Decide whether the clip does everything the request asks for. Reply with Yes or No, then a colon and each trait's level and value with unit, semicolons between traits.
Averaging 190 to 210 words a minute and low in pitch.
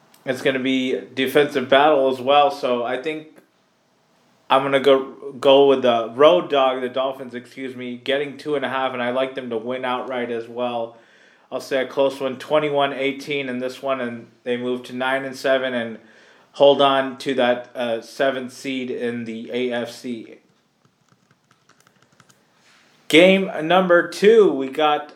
No: average, 165 wpm; low, 130 Hz